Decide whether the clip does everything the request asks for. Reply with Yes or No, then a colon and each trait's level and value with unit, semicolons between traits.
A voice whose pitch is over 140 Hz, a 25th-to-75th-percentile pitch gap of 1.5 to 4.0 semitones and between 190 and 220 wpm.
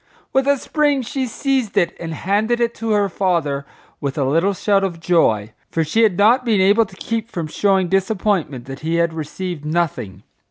No: high, 190 Hz; wide, 5.6 semitones; average, 195 wpm